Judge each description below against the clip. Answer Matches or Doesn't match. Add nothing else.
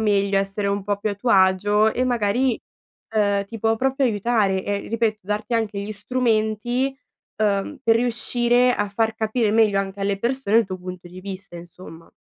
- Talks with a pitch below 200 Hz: Doesn't match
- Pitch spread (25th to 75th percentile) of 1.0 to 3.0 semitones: Matches